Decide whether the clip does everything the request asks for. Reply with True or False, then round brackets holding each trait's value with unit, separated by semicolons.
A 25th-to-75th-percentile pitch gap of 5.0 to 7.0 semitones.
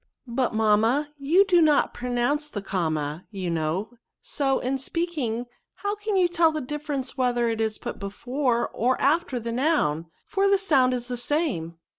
True (5.3 semitones)